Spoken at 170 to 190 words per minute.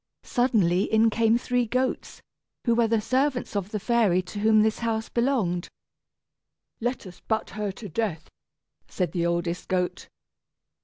No: average, 150 wpm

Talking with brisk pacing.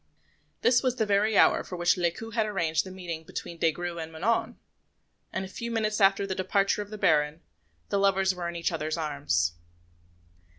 No: average, 195 wpm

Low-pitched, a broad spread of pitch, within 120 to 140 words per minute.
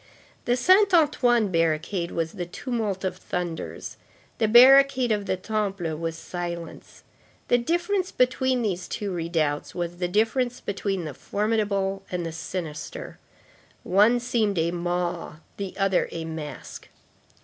No: high, 195 Hz; wide, 5.8 semitones; slow, 135 wpm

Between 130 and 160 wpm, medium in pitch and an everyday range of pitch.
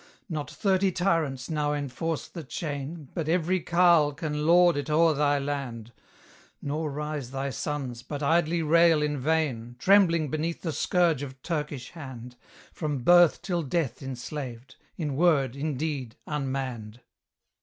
Yes: average, 145 wpm; medium, 150 Hz; average, 3.6 semitones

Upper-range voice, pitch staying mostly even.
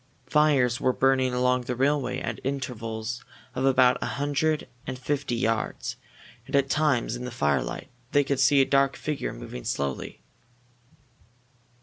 No: low, 130 Hz; narrow, 2.1 semitones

